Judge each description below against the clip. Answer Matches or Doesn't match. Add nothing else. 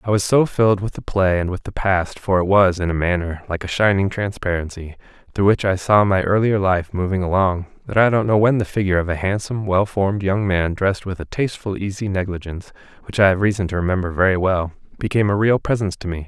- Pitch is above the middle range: Doesn't match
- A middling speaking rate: Doesn't match